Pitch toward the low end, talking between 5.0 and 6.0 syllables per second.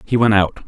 Yes: low, 105 Hz; 5.8 syllables/s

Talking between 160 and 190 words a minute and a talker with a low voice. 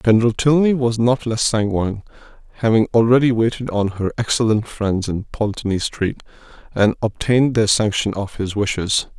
No: average, 150 wpm; low, 110 Hz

